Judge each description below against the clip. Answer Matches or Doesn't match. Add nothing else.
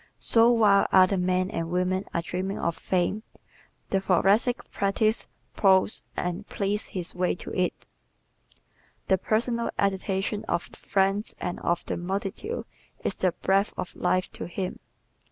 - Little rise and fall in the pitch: Matches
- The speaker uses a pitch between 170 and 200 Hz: Matches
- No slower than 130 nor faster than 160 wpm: Matches